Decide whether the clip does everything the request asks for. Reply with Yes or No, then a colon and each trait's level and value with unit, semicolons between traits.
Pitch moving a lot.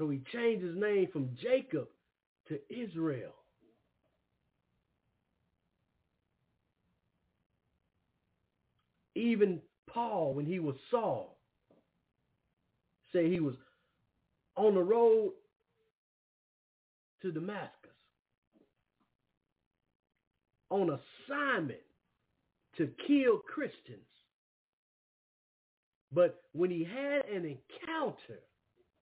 Yes: wide, 8.5 semitones